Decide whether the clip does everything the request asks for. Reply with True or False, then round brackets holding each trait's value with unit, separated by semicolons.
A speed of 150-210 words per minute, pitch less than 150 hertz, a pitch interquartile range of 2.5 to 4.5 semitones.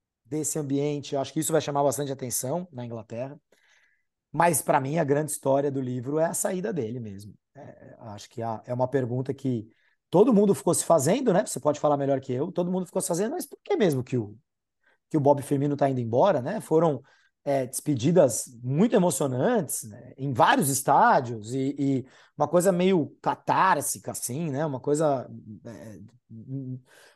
True (185 wpm; 140 Hz; 4.1 semitones)